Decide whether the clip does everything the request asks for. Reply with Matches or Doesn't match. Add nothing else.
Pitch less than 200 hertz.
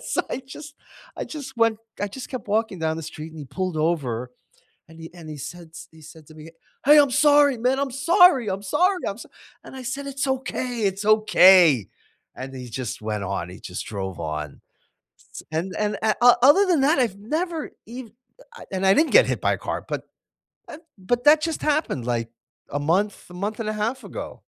Doesn't match